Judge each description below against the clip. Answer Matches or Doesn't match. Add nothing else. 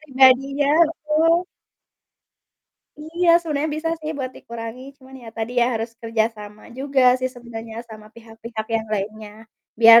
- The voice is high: Matches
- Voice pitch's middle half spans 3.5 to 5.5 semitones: Matches